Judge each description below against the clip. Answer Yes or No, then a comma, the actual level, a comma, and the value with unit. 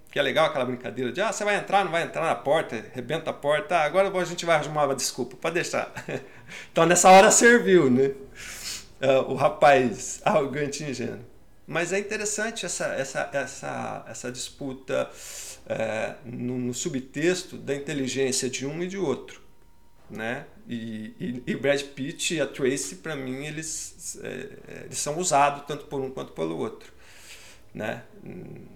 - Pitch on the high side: No, medium, 145 Hz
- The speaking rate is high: No, average, 165 wpm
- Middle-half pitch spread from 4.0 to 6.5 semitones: Yes, average, 5.2 semitones